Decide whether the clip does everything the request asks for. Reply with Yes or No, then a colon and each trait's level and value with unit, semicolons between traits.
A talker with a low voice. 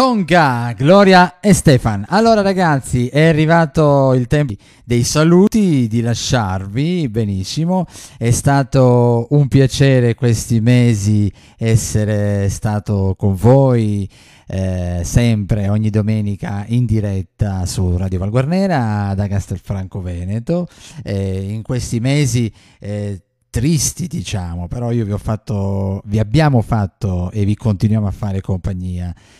Yes: low, 115 Hz